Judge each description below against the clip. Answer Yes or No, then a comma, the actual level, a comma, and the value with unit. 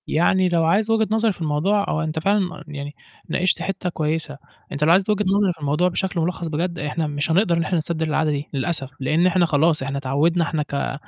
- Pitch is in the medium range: Yes, medium, 165 Hz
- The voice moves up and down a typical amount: Yes, average, 3.5 semitones